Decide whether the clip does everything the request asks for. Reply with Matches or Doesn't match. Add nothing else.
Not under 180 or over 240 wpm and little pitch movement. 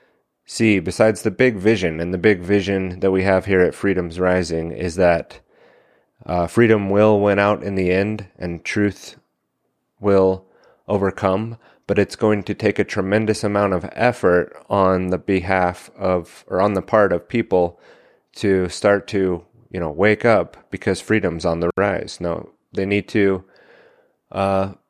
Doesn't match